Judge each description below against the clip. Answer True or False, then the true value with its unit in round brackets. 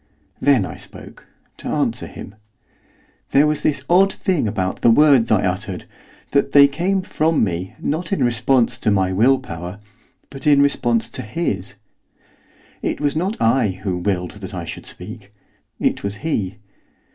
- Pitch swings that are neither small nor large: False (7.1 semitones)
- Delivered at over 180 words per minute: False (160 wpm)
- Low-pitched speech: True (120 Hz)